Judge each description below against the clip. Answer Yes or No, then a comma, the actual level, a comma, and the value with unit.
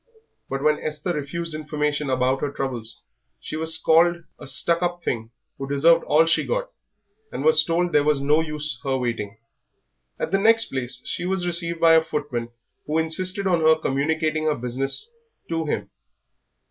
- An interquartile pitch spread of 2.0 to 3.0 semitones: No, average, 3.5 semitones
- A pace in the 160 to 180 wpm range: Yes, average, 170 wpm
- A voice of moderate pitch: Yes, medium, 155 Hz